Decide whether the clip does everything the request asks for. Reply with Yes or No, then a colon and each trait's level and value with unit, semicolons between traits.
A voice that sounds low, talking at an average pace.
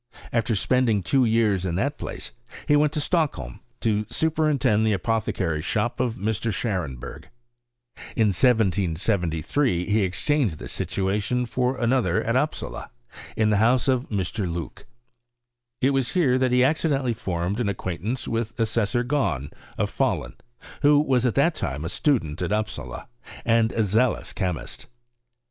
Yes: low, 110 Hz; average, 150 wpm